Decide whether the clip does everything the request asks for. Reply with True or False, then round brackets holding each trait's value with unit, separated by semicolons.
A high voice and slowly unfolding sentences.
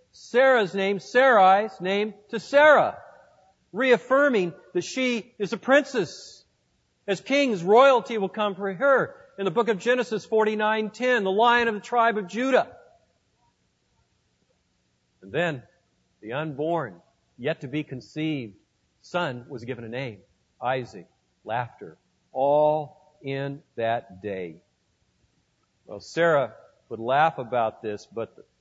True (195 Hz; 125 wpm)